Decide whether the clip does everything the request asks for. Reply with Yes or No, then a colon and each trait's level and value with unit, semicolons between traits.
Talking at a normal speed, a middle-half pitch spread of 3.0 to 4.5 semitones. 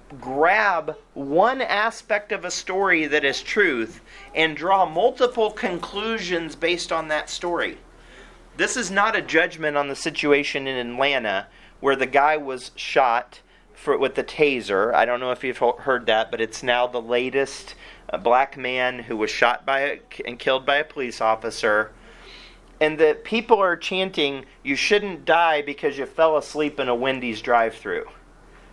No: average, 165 wpm; wide, 5.6 semitones